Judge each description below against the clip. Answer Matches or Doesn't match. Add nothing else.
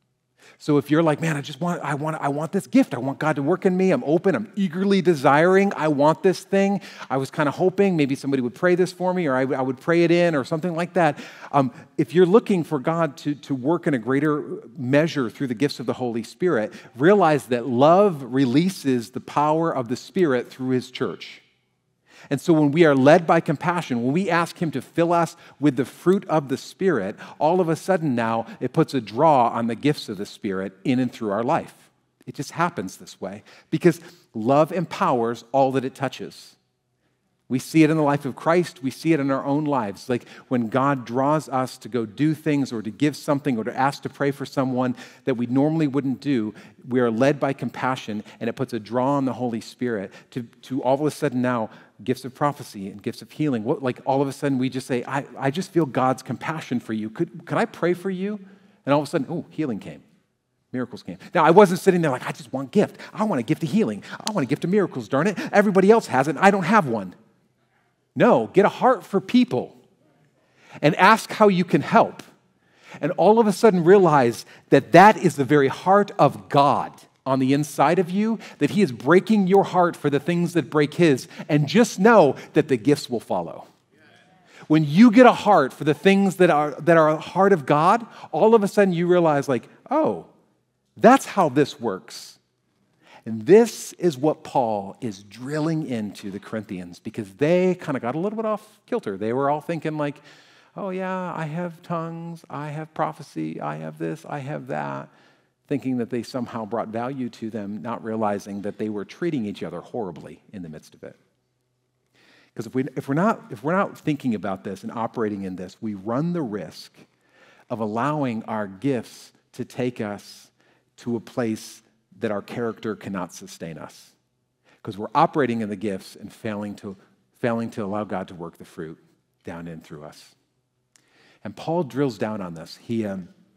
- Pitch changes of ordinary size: Doesn't match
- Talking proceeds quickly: Matches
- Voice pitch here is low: Doesn't match